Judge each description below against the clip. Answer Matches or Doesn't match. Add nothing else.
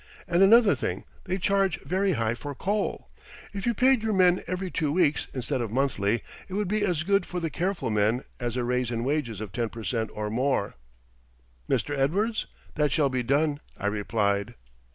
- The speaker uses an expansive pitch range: Matches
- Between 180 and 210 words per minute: Matches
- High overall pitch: Doesn't match